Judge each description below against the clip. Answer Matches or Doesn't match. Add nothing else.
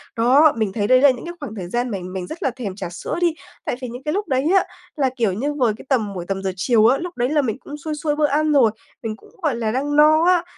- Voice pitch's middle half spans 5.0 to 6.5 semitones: Matches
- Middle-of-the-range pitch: Doesn't match